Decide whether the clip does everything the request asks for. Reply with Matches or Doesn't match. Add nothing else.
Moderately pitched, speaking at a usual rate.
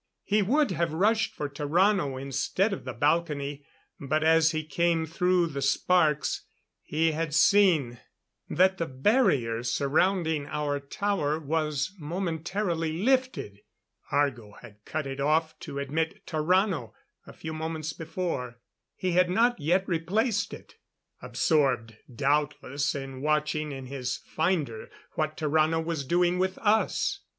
Doesn't match